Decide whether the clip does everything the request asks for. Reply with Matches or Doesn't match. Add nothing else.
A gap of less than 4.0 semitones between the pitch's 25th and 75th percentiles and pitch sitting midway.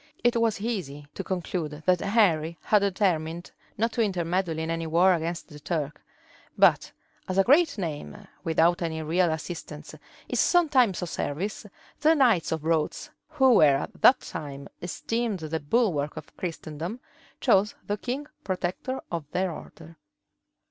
Doesn't match